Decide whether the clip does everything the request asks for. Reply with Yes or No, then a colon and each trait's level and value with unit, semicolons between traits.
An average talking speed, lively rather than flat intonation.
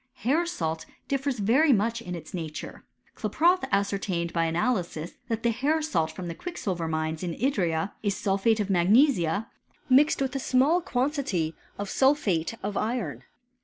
Yes: average, 155 wpm; wide, 7.7 semitones